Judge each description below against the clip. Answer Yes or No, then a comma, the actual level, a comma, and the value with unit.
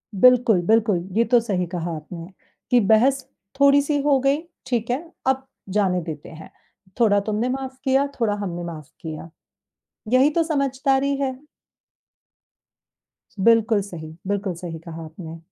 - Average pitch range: No, wide, 7.2 semitones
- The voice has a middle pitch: No, high, 225 Hz